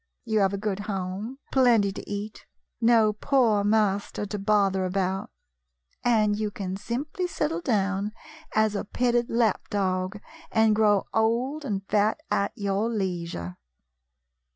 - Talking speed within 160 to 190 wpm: No, slow, 135 wpm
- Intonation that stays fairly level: Yes, narrow, 2.3 semitones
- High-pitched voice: Yes, high, 210 Hz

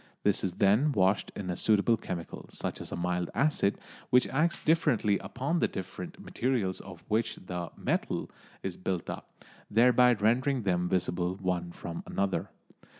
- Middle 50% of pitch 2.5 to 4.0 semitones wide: No, wide, 5.4 semitones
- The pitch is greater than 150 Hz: No, low, 100 Hz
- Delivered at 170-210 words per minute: No, average, 155 wpm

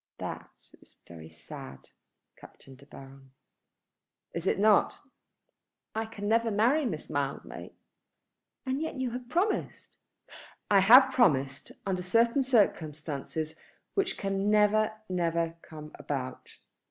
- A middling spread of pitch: No, wide, 7.4 semitones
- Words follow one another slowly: Yes, slow, 115 wpm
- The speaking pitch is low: No, high, 195 Hz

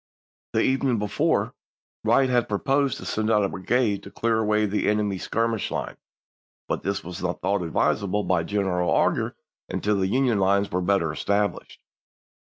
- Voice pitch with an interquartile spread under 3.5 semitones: Yes, average, 2.9 semitones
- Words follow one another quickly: No, average, 165 wpm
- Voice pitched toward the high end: No, low, 105 Hz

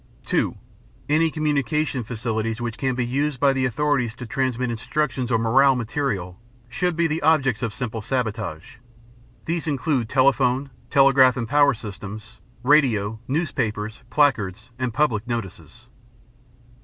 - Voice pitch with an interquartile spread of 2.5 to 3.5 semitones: No, average, 4.1 semitones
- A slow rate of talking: Yes, slow, 130 wpm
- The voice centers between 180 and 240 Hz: No, low, 125 Hz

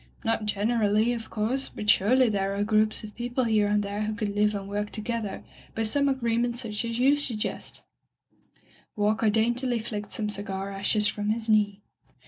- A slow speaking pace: No, average, 175 wpm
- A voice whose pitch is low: No, high, 215 Hz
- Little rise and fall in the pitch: Yes, narrow, 2.1 semitones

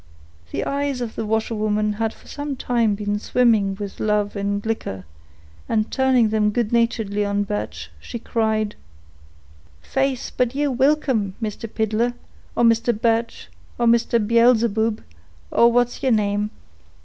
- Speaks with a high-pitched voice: Yes, high, 225 Hz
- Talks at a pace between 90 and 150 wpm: Yes, average, 140 wpm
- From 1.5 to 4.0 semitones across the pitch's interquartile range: Yes, narrow, 2.4 semitones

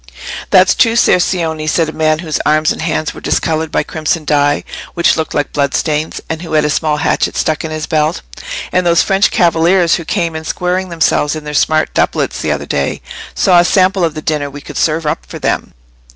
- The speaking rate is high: Yes, fast, 220 wpm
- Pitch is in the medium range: Yes, medium, 160 Hz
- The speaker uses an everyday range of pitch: No, narrow, 1.9 semitones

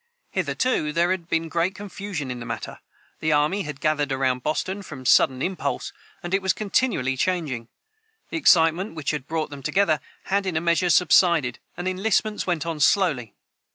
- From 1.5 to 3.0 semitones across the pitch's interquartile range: No, average, 4.8 semitones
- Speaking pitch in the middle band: Yes, medium, 165 Hz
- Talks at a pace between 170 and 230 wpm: Yes, average, 175 wpm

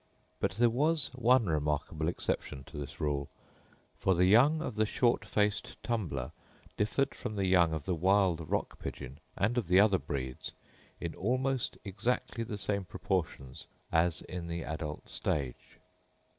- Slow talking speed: No, average, 155 wpm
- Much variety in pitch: Yes, wide, 6.6 semitones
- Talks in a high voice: No, very low, 95 Hz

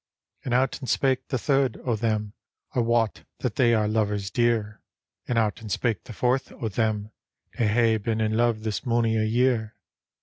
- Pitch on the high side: No, low, 115 Hz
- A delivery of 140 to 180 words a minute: No, average, 200 wpm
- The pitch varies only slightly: Yes, narrow, 2.0 semitones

